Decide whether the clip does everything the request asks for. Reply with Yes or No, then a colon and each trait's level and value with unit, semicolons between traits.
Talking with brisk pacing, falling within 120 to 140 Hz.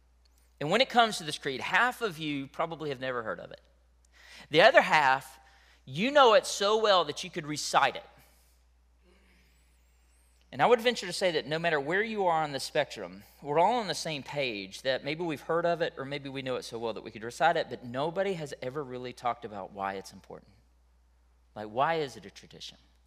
Yes: fast, 220 wpm; low, 135 Hz